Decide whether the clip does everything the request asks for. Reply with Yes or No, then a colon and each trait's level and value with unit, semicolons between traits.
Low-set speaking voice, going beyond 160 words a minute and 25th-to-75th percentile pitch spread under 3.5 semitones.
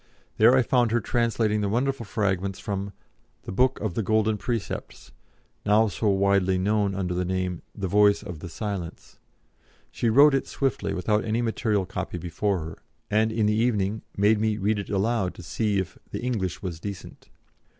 Yes: low, 105 Hz; average, 180 wpm; average, 2.7 semitones